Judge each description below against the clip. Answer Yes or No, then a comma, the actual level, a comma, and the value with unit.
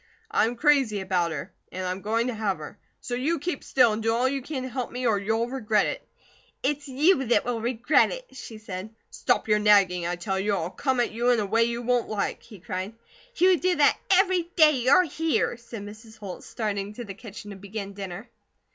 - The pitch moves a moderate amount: Yes, average, 4.6 semitones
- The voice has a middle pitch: No, high, 225 Hz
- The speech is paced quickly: Yes, fast, 225 wpm